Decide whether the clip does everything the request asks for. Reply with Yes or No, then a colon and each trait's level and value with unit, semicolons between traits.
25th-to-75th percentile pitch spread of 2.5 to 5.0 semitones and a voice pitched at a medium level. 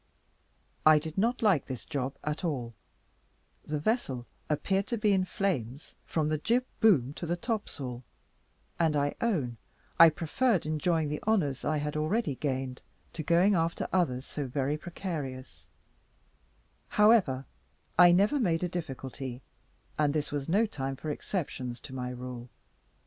No: wide, 5.5 semitones; medium, 155 Hz